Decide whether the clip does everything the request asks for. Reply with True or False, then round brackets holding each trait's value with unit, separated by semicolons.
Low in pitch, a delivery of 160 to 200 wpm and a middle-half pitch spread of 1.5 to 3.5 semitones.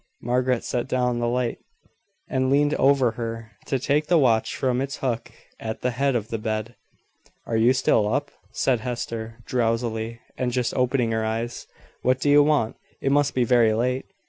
True (125 Hz; 180 wpm; 2.5 semitones)